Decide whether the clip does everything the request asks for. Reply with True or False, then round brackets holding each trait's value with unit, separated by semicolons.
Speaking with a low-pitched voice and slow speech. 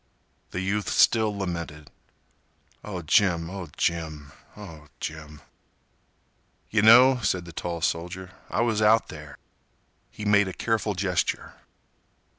True (95 Hz; 110 wpm)